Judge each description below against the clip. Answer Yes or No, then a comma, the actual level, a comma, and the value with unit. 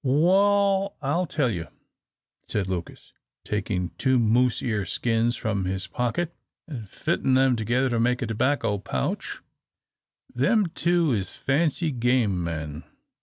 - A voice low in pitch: Yes, low, 125 Hz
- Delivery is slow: Yes, slow, 130 wpm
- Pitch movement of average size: No, wide, 6.1 semitones